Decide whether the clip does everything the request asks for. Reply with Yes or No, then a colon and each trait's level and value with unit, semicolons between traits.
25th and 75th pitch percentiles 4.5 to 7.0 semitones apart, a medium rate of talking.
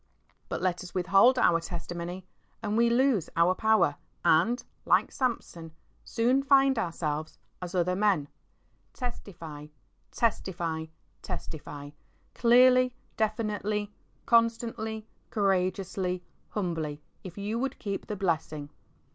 No: average, 5.2 semitones; slow, 115 wpm